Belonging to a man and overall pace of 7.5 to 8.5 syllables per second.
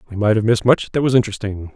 Yes: male; 7.7 syllables/s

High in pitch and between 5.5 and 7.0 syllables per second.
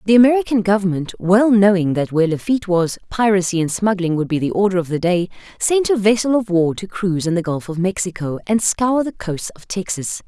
Yes: high, 195 Hz; 5.7 syllables/s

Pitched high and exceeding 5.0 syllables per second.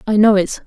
Yes: high, 205 Hz; 6.0 syllables/s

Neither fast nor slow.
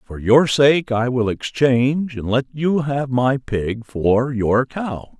Yes: average, 175 wpm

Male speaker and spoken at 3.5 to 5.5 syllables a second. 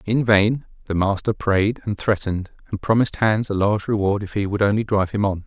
No: male; 5.9 syllables/s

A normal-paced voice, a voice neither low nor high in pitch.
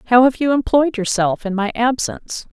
No: average, 185 wpm; high, 235 Hz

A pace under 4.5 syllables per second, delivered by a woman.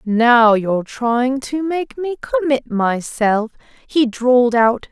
Yes: 3.5 syllables/s; female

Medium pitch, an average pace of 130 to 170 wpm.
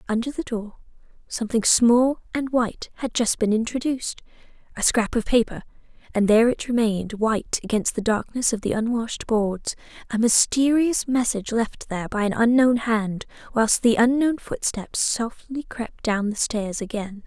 No: high, 230 Hz; average, 150 wpm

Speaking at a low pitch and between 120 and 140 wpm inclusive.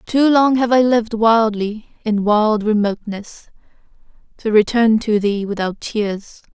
No: high, 220 Hz; slow, 135 wpm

